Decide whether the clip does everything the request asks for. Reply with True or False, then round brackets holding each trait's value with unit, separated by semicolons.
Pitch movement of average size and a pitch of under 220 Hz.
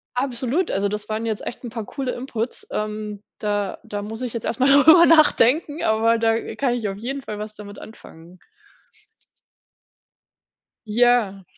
False (3.2 semitones; 225 Hz)